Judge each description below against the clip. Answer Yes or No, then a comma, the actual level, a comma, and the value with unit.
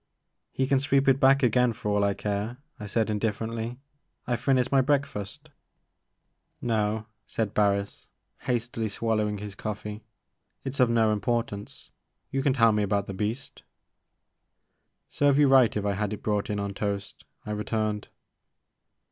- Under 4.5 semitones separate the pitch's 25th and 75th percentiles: Yes, average, 3.4 semitones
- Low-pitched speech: Yes, low, 110 Hz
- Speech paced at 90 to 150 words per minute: No, average, 165 wpm